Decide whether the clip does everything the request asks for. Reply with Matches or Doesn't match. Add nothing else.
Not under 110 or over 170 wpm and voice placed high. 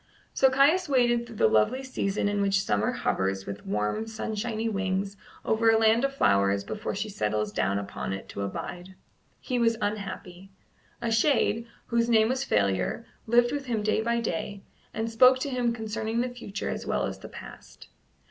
Doesn't match